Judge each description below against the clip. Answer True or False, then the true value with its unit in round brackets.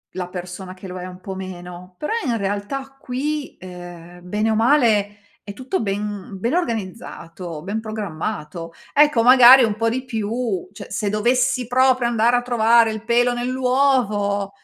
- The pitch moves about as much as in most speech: True (4.8 semitones)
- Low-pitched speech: False (220 Hz)